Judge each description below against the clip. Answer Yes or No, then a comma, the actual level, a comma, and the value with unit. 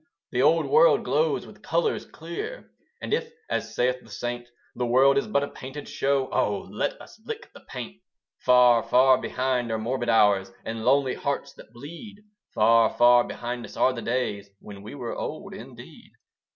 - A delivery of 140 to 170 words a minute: No, average, 180 wpm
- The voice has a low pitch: Yes, low, 125 Hz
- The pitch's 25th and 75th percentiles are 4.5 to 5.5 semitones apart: No, average, 3.4 semitones